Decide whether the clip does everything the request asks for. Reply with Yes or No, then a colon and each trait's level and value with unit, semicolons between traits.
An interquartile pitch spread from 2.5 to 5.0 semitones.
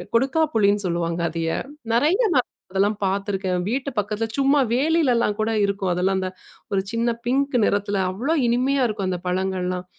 No: wide, 5.4 semitones